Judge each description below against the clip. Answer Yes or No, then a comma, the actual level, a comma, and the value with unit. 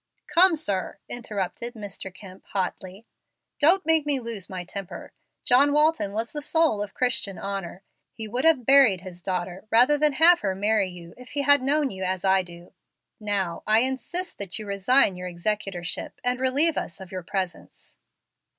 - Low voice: No, high, 210 Hz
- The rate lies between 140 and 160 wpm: No, average, 175 wpm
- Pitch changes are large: Yes, wide, 6.5 semitones